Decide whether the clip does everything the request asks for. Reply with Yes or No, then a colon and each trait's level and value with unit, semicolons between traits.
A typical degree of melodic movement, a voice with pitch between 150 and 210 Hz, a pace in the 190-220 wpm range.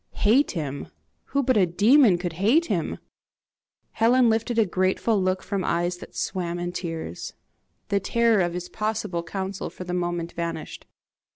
No: average, 4.2 semitones; medium, 185 Hz; average, 160 wpm